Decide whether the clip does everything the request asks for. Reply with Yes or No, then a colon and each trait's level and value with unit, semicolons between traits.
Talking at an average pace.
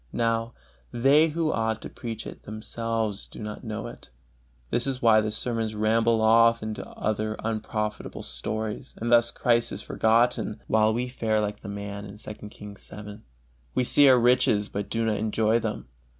Yes: average, 175 wpm